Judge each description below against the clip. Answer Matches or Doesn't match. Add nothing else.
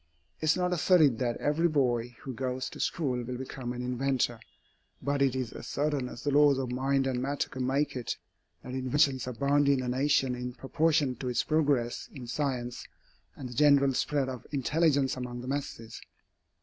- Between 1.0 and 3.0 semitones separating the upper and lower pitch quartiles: Matches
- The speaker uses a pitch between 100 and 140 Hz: Matches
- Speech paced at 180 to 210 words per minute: Matches